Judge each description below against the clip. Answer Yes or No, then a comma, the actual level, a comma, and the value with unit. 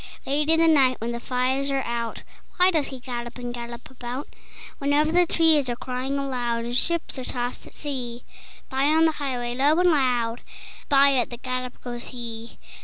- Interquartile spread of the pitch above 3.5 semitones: No, average, 3.0 semitones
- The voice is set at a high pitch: Yes, very high, 255 Hz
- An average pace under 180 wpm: No, average, 190 wpm